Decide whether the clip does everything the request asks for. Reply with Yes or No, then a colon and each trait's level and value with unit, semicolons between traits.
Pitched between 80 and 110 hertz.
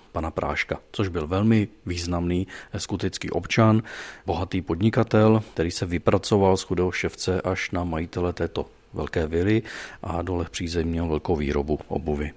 Yes: very low, 90 Hz